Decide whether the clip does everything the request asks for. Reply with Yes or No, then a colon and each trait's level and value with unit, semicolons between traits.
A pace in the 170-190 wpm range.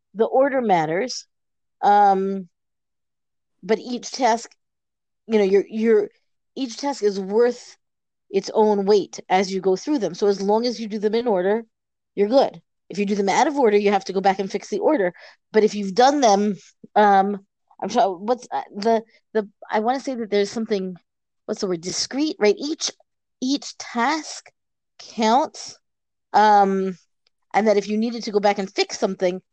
Yes: average, 185 wpm